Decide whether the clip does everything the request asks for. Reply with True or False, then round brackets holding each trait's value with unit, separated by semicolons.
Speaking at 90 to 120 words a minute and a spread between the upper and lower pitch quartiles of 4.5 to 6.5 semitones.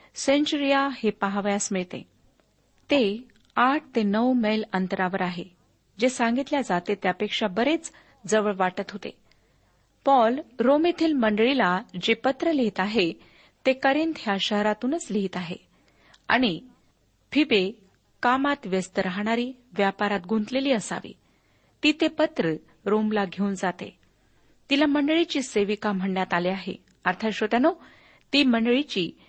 True (115 wpm; 5.5 semitones)